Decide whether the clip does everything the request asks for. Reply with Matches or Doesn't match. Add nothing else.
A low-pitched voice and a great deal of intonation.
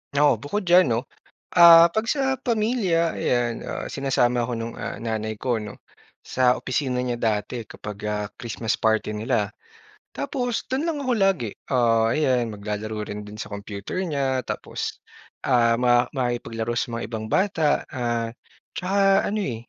Matches